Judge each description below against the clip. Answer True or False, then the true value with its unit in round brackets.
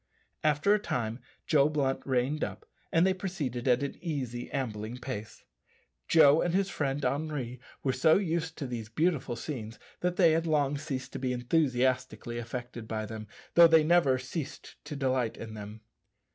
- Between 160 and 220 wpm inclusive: True (170 wpm)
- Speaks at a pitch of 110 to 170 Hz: True (135 Hz)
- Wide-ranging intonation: False (4.4 semitones)